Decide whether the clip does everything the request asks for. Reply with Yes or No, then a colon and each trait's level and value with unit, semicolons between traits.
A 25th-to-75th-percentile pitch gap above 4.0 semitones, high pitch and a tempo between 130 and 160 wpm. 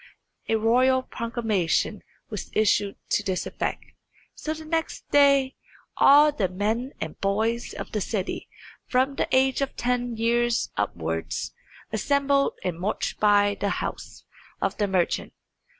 Yes: average, 4.6 semitones; high, 230 Hz; slow, 135 wpm